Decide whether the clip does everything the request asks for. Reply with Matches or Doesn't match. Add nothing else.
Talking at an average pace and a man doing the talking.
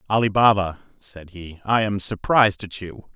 Matches